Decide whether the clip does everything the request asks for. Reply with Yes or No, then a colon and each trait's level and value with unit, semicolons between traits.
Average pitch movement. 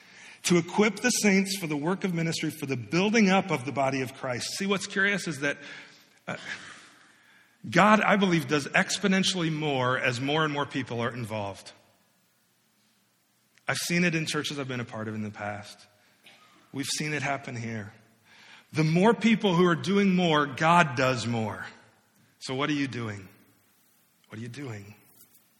No: wide, 7.0 semitones